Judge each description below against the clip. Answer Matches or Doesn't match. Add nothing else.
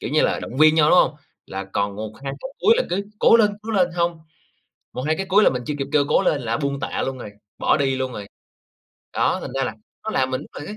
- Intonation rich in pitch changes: Matches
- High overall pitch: Doesn't match